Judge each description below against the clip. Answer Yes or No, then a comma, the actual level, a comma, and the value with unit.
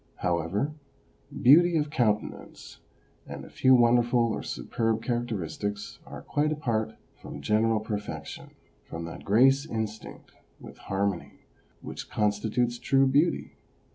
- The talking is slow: Yes, slow, 125 wpm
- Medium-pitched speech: No, low, 115 Hz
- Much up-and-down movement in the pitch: No, average, 4.1 semitones